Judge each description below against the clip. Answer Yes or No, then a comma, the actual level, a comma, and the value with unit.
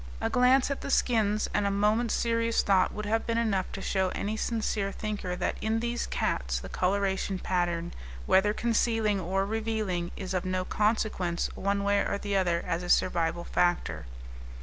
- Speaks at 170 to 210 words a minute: Yes, average, 175 wpm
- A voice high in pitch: Yes, high, 200 Hz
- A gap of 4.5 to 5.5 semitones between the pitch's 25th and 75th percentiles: No, average, 3.2 semitones